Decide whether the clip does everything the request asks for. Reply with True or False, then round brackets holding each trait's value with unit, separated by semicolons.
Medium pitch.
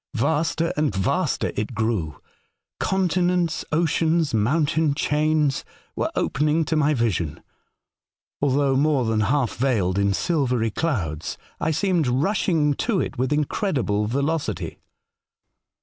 True (145 Hz)